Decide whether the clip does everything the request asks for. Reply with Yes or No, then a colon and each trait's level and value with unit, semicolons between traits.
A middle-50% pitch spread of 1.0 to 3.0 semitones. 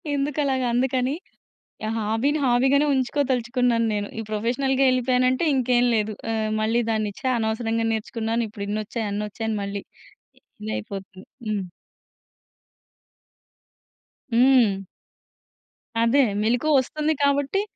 No: average, 3.5 semitones